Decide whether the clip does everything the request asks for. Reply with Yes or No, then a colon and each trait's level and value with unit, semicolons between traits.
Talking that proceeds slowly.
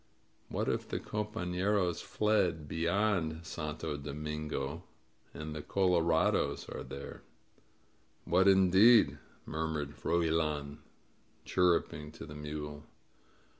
Yes: slow, 100 wpm